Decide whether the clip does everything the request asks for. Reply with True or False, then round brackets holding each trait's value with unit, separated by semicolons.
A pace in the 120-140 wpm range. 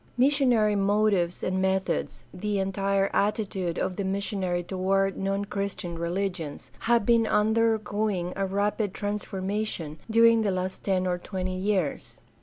True (135 wpm)